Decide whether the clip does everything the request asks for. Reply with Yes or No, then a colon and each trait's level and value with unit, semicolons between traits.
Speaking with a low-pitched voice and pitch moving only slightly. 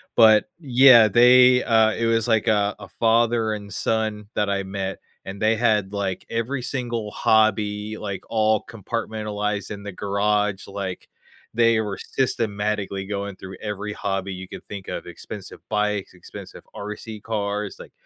Yes: low, 105 Hz; narrow, 1.9 semitones